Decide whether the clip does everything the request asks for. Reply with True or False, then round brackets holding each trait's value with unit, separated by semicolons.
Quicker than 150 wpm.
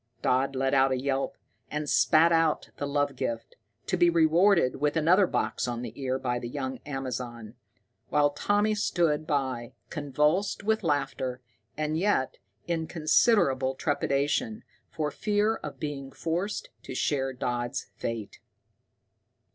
False (140 wpm)